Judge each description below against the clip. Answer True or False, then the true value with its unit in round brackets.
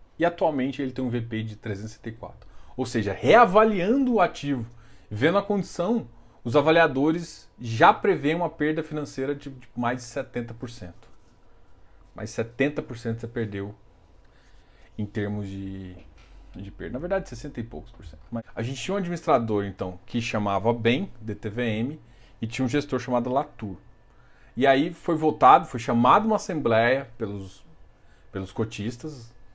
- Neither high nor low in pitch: False (120 Hz)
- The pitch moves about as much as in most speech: False (5.8 semitones)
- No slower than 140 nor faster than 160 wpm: True (145 wpm)